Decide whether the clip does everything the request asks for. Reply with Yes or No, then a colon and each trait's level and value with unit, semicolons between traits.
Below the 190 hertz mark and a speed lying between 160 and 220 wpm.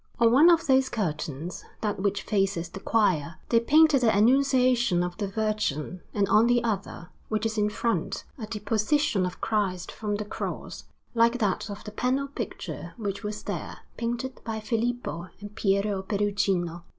No: high, 210 Hz; average, 165 wpm